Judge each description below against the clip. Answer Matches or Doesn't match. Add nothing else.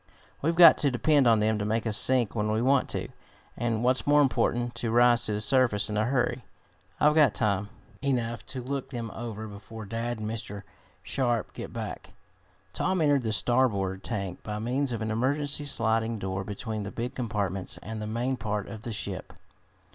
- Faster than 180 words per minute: Matches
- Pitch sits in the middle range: Doesn't match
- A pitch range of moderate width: Matches